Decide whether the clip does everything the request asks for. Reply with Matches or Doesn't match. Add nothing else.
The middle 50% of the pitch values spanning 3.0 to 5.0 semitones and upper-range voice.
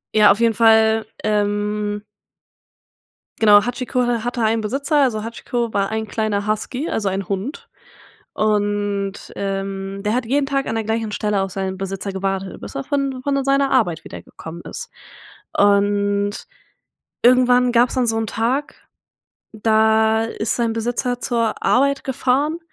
Matches